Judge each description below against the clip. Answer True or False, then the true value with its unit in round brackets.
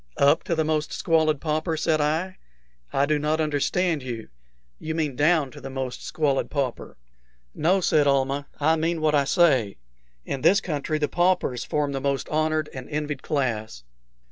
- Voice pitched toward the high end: False (150 Hz)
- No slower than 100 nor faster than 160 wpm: False (170 wpm)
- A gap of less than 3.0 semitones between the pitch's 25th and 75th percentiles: True (2.4 semitones)